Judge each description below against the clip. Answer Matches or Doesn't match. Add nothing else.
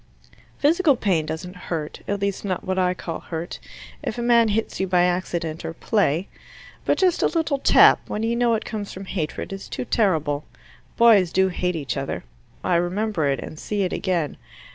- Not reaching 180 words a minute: Doesn't match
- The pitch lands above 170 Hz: Matches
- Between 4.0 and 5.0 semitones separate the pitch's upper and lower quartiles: Matches